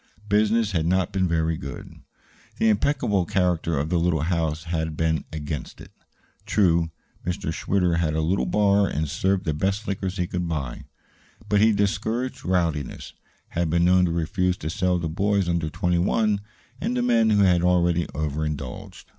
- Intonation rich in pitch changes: No, average, 3.6 semitones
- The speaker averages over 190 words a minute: No, average, 170 wpm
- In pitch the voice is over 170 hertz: No, very low, 90 Hz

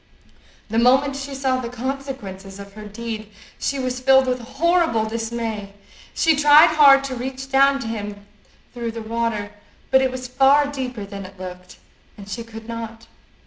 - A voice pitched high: Yes, high, 240 Hz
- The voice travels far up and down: No, average, 3.7 semitones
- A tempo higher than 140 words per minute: Yes, average, 170 wpm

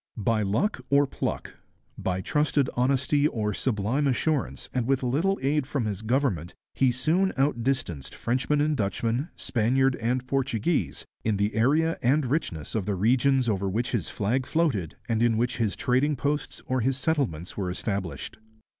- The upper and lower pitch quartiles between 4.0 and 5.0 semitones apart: Yes, average, 4.6 semitones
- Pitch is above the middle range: No, low, 125 Hz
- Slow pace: No, average, 160 wpm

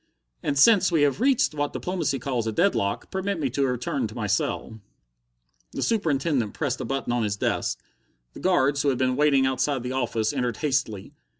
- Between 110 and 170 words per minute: No, average, 190 wpm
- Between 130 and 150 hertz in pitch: Yes, low, 135 Hz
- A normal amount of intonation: Yes, average, 3.8 semitones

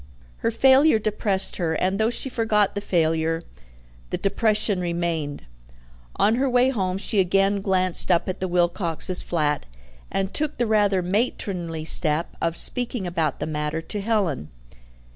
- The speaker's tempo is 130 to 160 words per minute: Yes, average, 150 wpm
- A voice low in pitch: No, high, 190 Hz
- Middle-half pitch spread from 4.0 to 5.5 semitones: Yes, average, 4.3 semitones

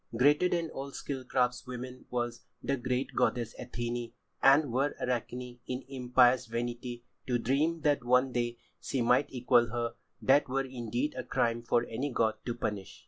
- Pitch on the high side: No, low, 125 Hz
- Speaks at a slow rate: No, average, 160 wpm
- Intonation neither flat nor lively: No, narrow, 2.0 semitones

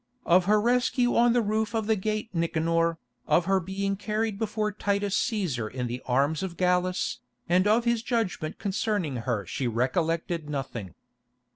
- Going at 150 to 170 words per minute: Yes, average, 160 wpm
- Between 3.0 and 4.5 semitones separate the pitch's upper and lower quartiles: No, average, 5.2 semitones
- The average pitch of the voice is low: No, high, 190 Hz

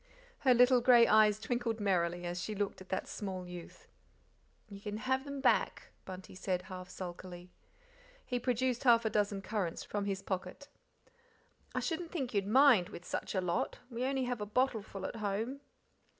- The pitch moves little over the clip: No, average, 4.8 semitones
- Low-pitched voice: No, high, 210 Hz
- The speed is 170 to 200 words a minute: Yes, average, 175 wpm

